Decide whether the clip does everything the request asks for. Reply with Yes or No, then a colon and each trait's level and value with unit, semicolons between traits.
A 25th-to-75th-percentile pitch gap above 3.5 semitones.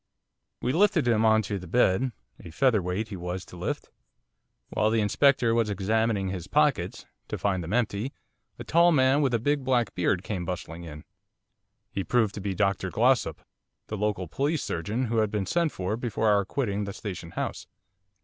Yes: average, 4.5 semitones